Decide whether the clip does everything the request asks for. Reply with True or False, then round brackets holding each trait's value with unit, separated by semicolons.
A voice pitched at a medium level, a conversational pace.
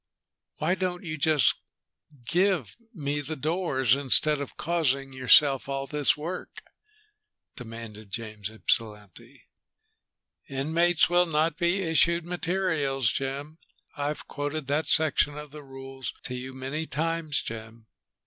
False (145 Hz; 120 wpm)